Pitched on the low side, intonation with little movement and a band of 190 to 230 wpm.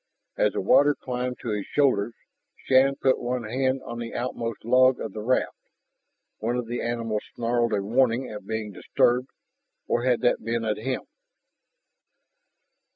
No: low, 120 Hz; narrow, 2.1 semitones; average, 160 wpm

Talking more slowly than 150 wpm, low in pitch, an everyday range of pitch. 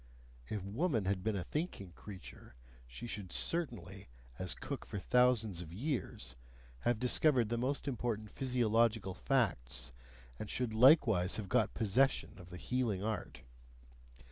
Yes: average, 140 wpm; low, 110 Hz; average, 4.9 semitones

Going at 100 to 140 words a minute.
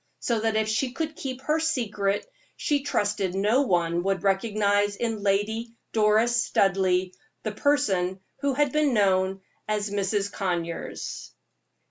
Yes: slow, 135 wpm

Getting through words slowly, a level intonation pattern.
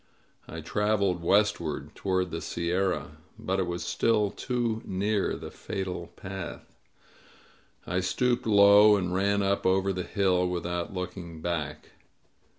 Yes: slow, 130 wpm; narrow, 2.2 semitones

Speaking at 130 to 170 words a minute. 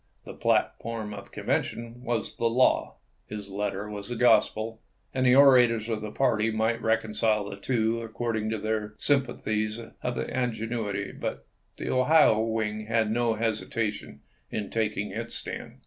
Yes: average, 150 wpm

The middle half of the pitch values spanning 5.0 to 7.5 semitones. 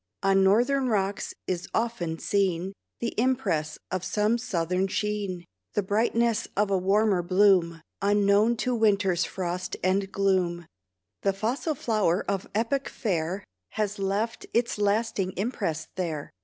No: average, 3.1 semitones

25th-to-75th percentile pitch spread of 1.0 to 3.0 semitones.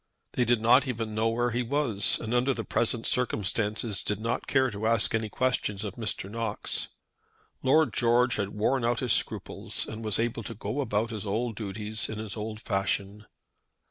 Yes: narrow, 2.4 semitones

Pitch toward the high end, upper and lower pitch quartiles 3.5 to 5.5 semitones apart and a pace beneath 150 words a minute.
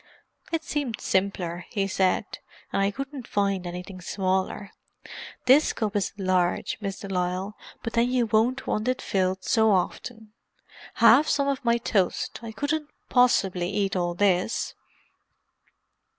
Yes: high, 205 Hz; average, 4.6 semitones; slow, 135 wpm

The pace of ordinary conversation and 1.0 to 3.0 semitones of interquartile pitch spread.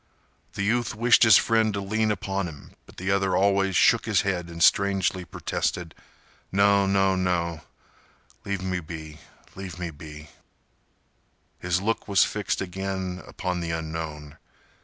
No: slow, 130 wpm; average, 2.7 semitones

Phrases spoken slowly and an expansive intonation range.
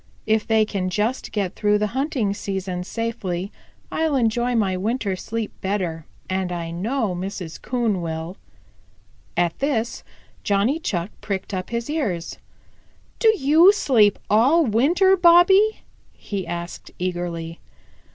Yes: slow, 130 wpm; wide, 5.7 semitones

